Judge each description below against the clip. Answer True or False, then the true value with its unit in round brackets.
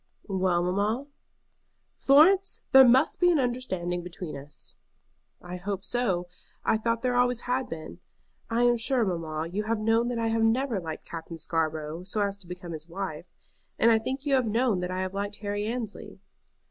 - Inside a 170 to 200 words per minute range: True (185 wpm)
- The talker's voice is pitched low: False (205 Hz)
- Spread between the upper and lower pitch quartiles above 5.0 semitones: True (5.5 semitones)